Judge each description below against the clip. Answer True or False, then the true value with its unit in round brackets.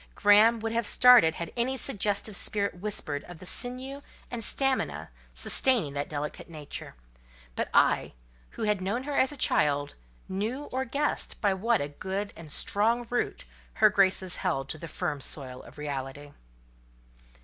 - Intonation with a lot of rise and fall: True (7.5 semitones)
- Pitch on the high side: True (200 Hz)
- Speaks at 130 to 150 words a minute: False (160 wpm)